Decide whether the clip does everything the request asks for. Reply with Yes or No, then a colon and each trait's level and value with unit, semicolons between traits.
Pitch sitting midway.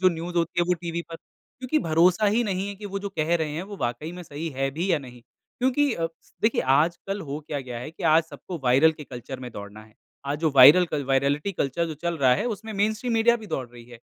Yes: medium, 165 Hz